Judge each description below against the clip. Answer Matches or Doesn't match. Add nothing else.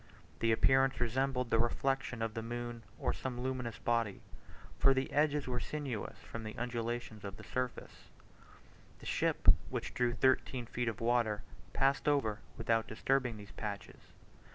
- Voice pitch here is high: Doesn't match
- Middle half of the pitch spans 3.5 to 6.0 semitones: Doesn't match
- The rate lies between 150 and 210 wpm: Matches